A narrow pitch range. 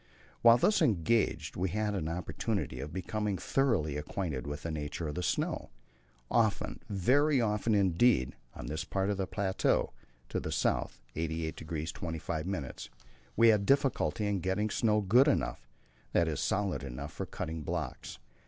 No: average, 5.3 semitones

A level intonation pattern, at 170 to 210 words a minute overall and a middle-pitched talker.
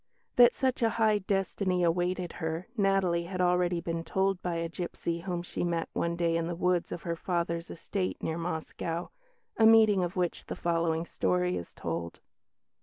Yes: narrow, 1.9 semitones; average, 180 wpm; medium, 175 Hz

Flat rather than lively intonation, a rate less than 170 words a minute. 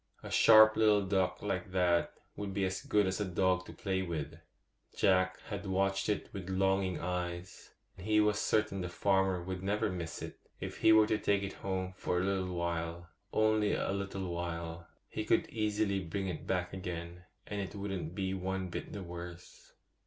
No: narrow, 2.1 semitones; average, 180 wpm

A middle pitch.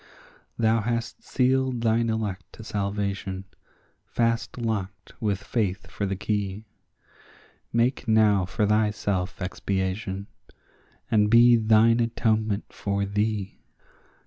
No: low, 105 Hz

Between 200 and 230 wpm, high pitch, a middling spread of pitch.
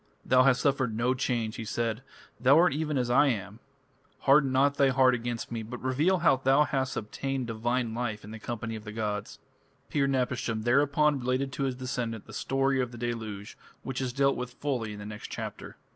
No: fast, 205 wpm; low, 125 Hz; average, 3.1 semitones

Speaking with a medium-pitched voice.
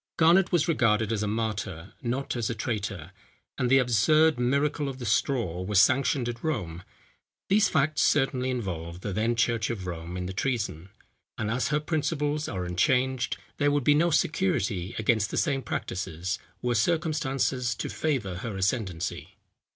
No: low, 120 Hz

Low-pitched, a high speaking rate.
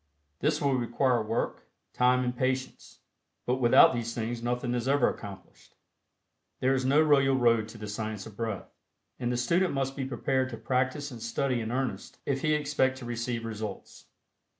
No: low, 125 Hz; average, 175 wpm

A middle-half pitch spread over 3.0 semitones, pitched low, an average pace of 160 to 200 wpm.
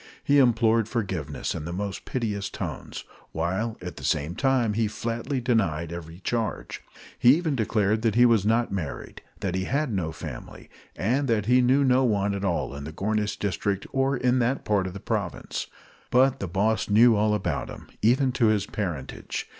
Yes: average, 4.2 semitones; low, 110 Hz; average, 180 wpm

